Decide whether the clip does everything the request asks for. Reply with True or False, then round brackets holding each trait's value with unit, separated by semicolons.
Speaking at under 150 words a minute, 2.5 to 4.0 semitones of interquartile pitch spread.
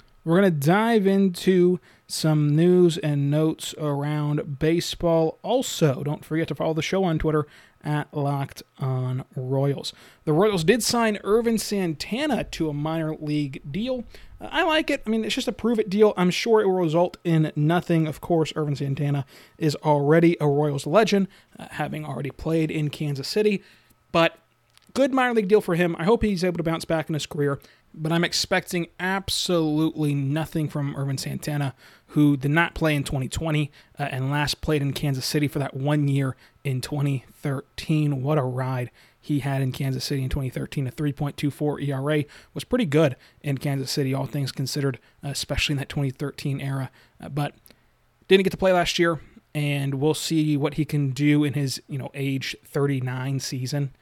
False (180 wpm; 3.4 semitones)